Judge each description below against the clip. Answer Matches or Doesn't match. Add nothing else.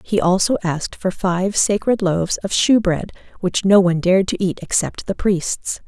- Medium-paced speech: Matches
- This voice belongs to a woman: Matches